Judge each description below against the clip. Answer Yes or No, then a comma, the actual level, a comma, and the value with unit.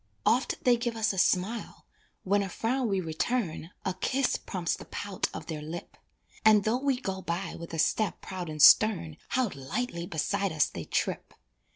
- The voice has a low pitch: No, high, 195 Hz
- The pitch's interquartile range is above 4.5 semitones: Yes, average, 5.2 semitones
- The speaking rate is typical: Yes, average, 185 wpm